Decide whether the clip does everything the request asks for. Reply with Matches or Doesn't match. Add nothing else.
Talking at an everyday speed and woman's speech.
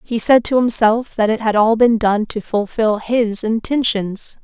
Matches